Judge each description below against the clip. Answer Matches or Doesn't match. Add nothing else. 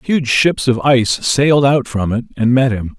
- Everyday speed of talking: Doesn't match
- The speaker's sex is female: Doesn't match